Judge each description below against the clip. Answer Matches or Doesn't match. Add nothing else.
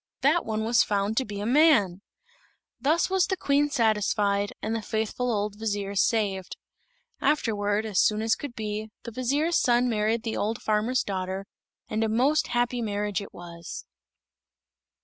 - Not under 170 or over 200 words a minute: Doesn't match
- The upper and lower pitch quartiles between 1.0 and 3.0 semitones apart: Doesn't match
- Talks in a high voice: Matches